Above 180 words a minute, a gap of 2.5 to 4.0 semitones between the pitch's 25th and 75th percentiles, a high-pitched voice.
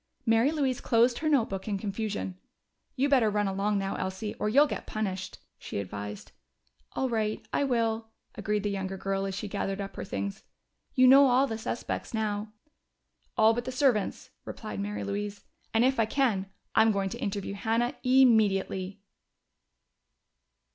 No: average, 160 wpm; average, 3.4 semitones; high, 215 Hz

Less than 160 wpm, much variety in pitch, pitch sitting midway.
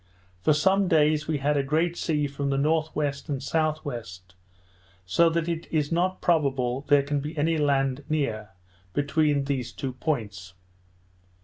No: average, 150 wpm; narrow, 2.5 semitones; medium, 145 Hz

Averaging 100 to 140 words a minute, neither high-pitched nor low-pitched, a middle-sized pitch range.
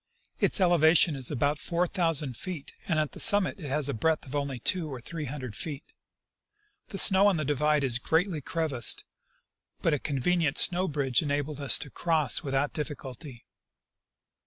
No: average, 175 wpm; medium, 150 Hz; average, 3.4 semitones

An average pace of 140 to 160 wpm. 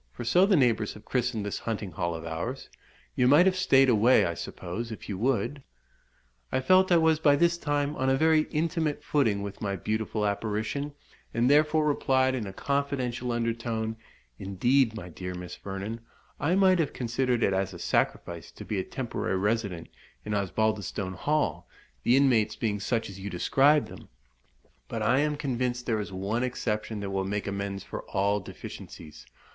No: average, 180 wpm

